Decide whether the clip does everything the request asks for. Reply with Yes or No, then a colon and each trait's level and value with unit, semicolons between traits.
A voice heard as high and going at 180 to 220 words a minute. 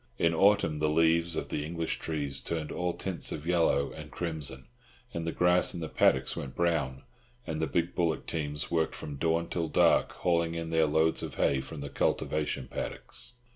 No: very low, 80 Hz; average, 190 wpm